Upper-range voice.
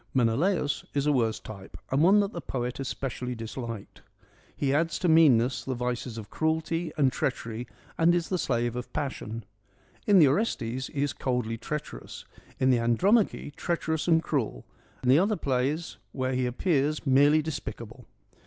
No: low, 135 Hz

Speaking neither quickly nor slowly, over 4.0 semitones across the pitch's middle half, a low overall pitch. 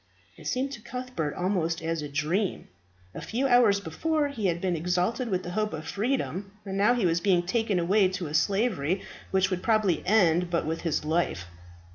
No: average, 190 wpm; average, 4.6 semitones; high, 190 Hz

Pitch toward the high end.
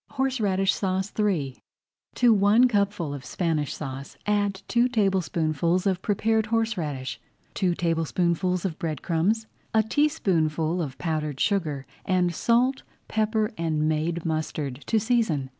No: medium, 180 Hz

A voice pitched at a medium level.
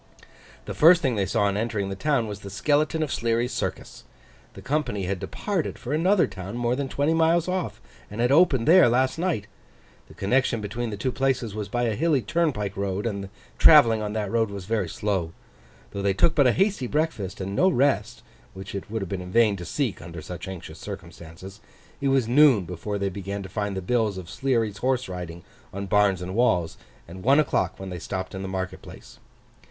No: low, 110 Hz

